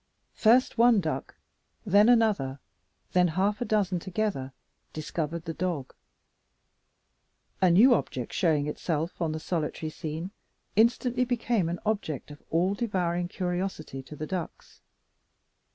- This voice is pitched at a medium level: Yes, medium, 180 Hz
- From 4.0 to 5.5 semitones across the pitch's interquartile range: Yes, average, 5.1 semitones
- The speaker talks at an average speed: No, slow, 125 wpm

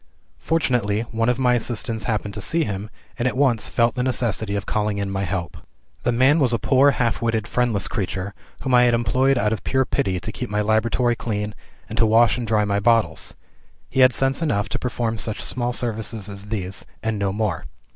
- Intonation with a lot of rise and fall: No, average, 3.1 semitones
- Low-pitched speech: Yes, low, 115 Hz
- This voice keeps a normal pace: No, fast, 210 wpm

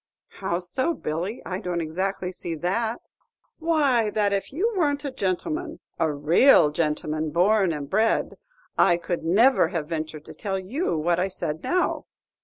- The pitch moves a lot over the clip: Yes, wide, 6.7 semitones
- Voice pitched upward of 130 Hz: Yes, medium, 185 Hz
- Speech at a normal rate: Yes, average, 160 wpm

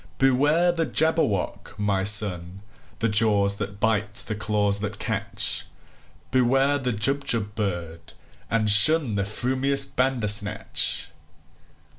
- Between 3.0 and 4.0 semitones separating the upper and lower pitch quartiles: No, average, 4.6 semitones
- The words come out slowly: Yes, slow, 95 wpm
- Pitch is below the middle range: Yes, low, 105 Hz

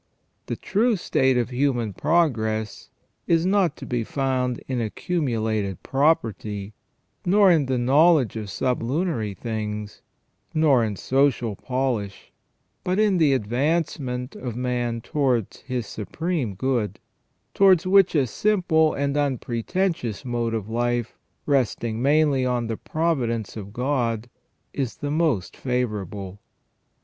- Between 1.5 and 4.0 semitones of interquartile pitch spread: No, average, 5.3 semitones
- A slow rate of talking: Yes, slow, 125 wpm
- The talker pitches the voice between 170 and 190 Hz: No, low, 125 Hz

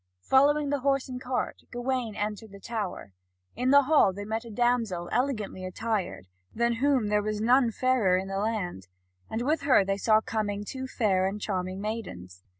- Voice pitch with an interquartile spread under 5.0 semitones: Yes, average, 4.3 semitones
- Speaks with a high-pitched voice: Yes, high, 220 Hz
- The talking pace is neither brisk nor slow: Yes, average, 180 wpm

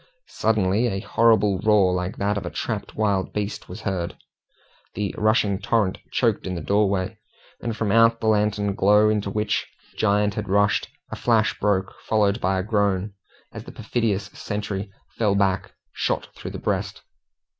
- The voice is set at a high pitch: No, low, 105 Hz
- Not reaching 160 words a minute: No, average, 165 wpm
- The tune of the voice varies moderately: No, narrow, 1.7 semitones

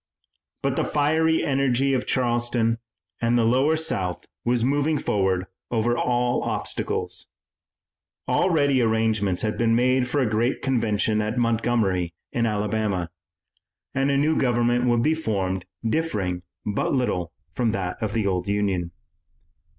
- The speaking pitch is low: Yes, low, 115 Hz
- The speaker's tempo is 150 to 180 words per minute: No, slow, 135 wpm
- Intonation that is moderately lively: Yes, average, 4.0 semitones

